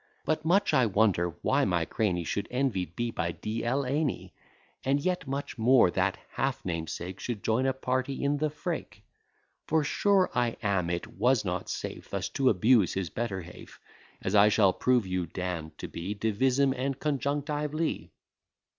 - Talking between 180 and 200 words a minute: No, average, 170 wpm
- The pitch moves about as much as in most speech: No, wide, 6.6 semitones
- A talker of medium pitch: No, low, 120 Hz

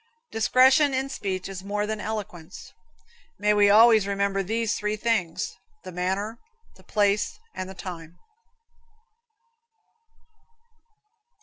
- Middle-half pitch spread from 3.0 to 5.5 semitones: No, narrow, 2.6 semitones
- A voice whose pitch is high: Yes, high, 205 Hz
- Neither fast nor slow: No, slow, 110 wpm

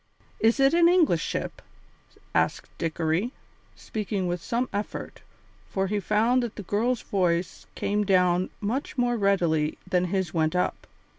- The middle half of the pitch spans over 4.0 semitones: Yes, average, 4.8 semitones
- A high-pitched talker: Yes, high, 200 Hz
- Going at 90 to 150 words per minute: Yes, average, 145 wpm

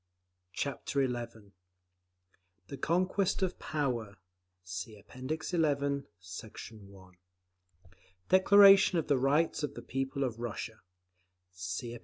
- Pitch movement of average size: No, wide, 6.3 semitones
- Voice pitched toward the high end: No, low, 135 Hz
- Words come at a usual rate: No, slow, 110 wpm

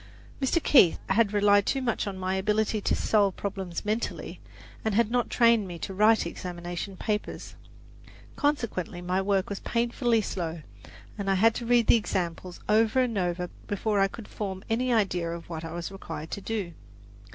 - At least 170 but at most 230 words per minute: Yes, average, 175 wpm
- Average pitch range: Yes, average, 3.7 semitones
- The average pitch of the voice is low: No, high, 200 Hz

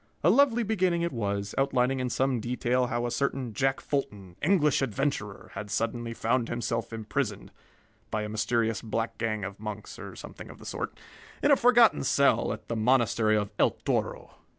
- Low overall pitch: Yes, low, 120 Hz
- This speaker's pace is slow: No, average, 175 wpm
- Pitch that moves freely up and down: No, average, 4.1 semitones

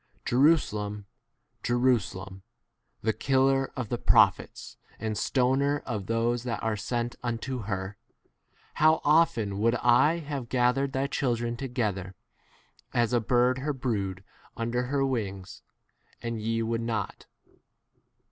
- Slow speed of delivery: Yes, slow, 130 wpm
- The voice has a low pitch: Yes, low, 120 Hz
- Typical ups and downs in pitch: Yes, average, 3.4 semitones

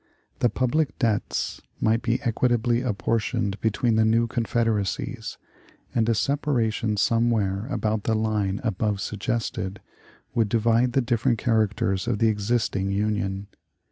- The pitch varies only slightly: Yes, narrow, 2.2 semitones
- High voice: No, low, 110 Hz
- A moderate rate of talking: No, slow, 125 wpm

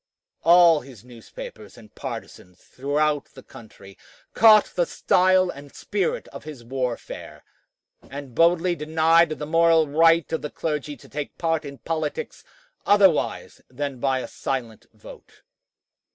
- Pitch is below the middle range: No, medium, 150 Hz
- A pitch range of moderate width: Yes, average, 3.9 semitones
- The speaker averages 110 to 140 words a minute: Yes, slow, 135 wpm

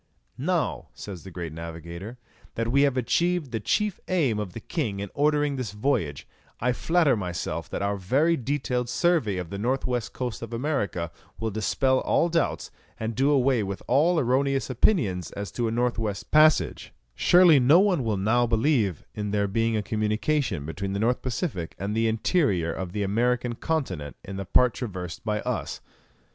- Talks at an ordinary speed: Yes, average, 180 wpm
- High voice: No, low, 115 Hz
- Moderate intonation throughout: No, wide, 5.7 semitones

